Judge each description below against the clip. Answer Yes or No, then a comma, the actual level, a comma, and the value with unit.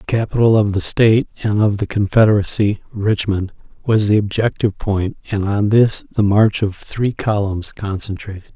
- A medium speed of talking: Yes, average, 160 wpm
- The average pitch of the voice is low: Yes, low, 105 Hz